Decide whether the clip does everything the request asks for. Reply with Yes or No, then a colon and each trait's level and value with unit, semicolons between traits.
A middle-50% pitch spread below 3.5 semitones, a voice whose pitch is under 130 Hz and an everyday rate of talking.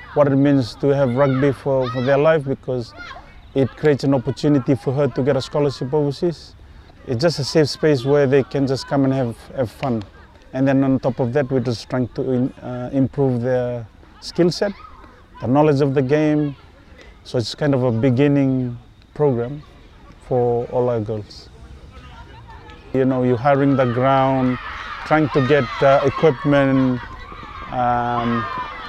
No: average, 2.9 semitones; low, 135 Hz; average, 165 wpm